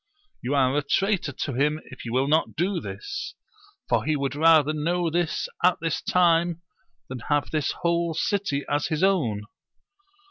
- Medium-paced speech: Yes, average, 170 wpm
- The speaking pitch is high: No, medium, 155 Hz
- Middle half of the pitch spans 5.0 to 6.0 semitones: No, average, 3.6 semitones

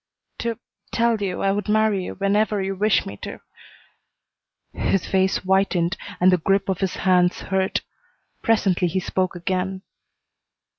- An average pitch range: No, narrow, 1.6 semitones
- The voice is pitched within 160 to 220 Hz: Yes, high, 190 Hz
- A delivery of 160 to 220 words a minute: No, average, 150 wpm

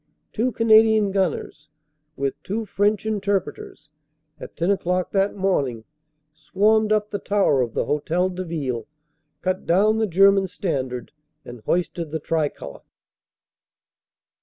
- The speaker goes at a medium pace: No, slow, 130 wpm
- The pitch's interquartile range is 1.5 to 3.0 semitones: No, average, 5.1 semitones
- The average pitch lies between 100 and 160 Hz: No, medium, 185 Hz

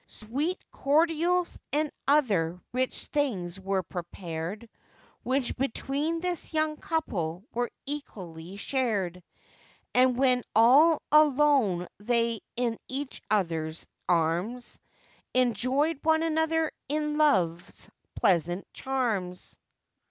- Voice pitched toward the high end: Yes, very high, 250 Hz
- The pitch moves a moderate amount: No, wide, 8.1 semitones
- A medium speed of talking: No, slow, 95 wpm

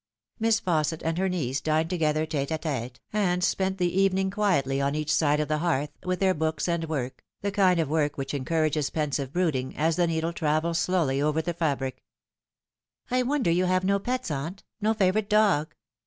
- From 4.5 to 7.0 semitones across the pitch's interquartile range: No, average, 3.8 semitones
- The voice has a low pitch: No, medium, 165 Hz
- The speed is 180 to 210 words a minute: Yes, average, 200 wpm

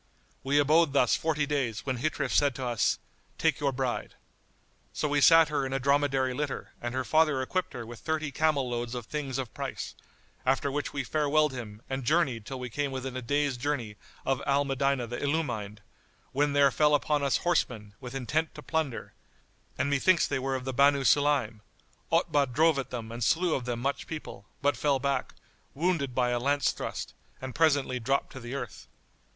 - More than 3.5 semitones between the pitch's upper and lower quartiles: No, average, 2.8 semitones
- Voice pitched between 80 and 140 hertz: Yes, low, 135 Hz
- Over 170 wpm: Yes, average, 195 wpm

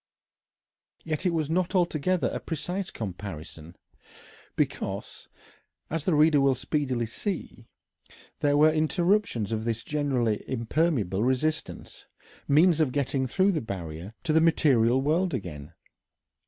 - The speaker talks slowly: Yes, slow, 125 wpm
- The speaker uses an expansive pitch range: Yes, wide, 6.2 semitones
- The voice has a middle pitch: Yes, medium, 145 Hz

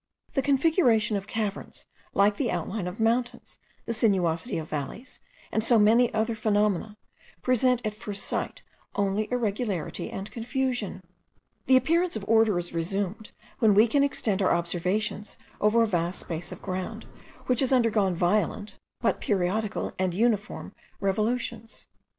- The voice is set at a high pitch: Yes, high, 215 Hz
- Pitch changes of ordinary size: Yes, average, 3.3 semitones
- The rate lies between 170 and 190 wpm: No, average, 145 wpm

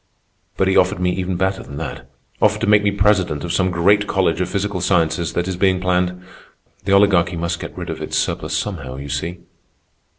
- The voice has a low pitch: Yes, very low, 90 Hz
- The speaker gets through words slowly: No, average, 195 wpm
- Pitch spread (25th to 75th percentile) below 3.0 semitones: Yes, narrow, 2.4 semitones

